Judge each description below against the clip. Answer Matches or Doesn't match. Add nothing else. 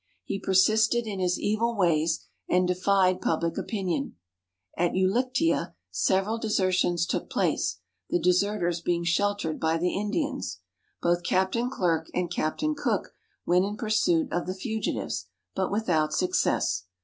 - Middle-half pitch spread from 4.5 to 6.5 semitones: Doesn't match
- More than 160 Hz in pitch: Matches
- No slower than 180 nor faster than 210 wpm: Doesn't match